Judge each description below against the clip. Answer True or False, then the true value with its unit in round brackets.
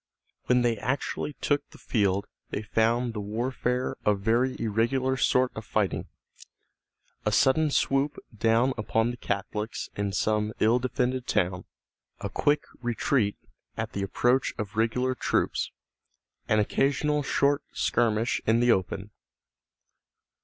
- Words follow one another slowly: True (130 wpm)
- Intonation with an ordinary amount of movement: True (3.3 semitones)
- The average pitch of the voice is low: True (115 Hz)